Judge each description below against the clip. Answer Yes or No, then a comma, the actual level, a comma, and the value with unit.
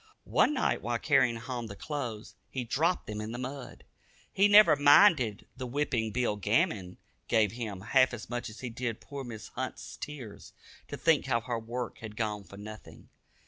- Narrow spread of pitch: No, average, 4.1 semitones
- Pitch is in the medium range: No, low, 120 Hz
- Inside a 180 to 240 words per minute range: Yes, average, 185 wpm